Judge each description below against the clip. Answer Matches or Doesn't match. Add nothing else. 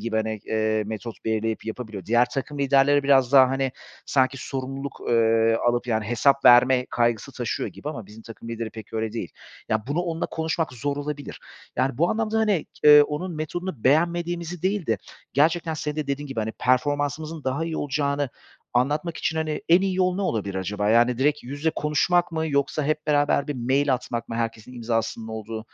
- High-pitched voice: Doesn't match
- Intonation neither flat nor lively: Matches